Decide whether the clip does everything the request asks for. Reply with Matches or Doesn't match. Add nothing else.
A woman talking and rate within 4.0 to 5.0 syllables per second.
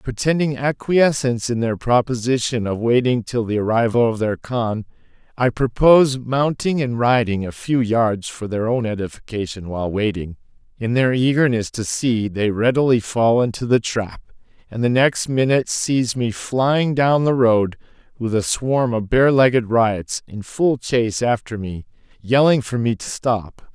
Doesn't match